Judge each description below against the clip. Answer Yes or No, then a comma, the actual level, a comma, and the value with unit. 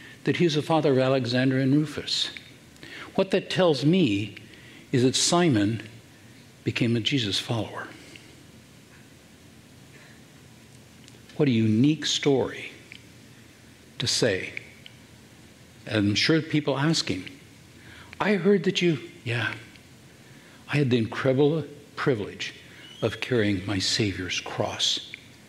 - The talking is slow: Yes, slow, 105 wpm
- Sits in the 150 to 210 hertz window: No, low, 130 Hz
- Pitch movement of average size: Yes, average, 4.6 semitones